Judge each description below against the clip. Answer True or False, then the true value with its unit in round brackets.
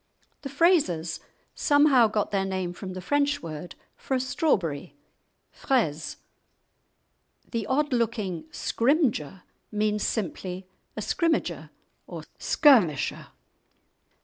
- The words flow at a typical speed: False (100 wpm)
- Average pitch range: False (7.6 semitones)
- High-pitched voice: True (215 Hz)